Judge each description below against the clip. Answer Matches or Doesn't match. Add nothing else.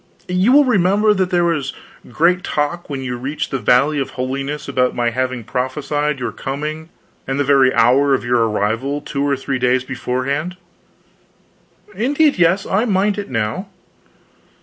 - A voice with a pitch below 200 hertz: Matches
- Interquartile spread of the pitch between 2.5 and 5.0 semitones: Doesn't match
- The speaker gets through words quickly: Doesn't match